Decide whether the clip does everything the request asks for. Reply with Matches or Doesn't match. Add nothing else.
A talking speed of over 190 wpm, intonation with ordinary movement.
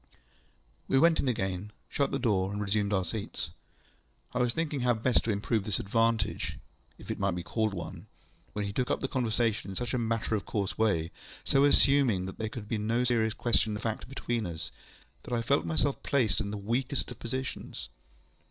Matches